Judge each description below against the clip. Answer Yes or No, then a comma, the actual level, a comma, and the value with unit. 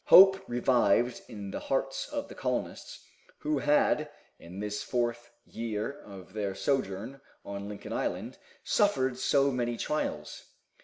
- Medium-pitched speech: No, low, 120 Hz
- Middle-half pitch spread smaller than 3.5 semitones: No, average, 4.9 semitones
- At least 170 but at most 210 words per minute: No, slow, 135 wpm